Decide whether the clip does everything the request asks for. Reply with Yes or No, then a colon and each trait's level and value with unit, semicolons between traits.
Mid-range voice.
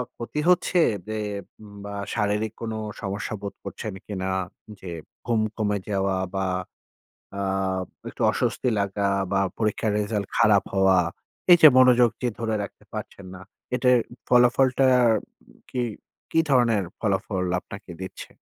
No: low, 105 Hz